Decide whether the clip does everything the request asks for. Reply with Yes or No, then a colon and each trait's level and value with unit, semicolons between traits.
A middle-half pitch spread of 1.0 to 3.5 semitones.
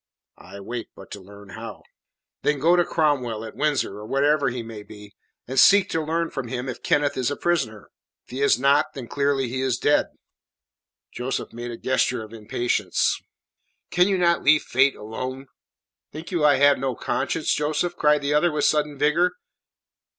No: average, 3.9 semitones